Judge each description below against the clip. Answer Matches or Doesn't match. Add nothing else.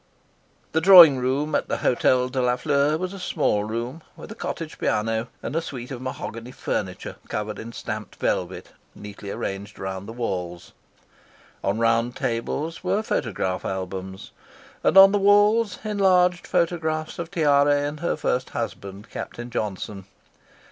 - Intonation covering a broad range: Matches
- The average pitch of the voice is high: Doesn't match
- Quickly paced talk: Doesn't match